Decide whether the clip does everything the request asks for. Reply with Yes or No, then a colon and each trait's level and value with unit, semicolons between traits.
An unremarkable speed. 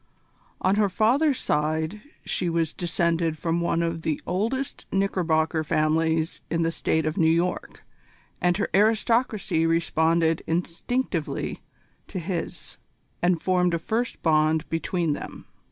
No: slow, 130 wpm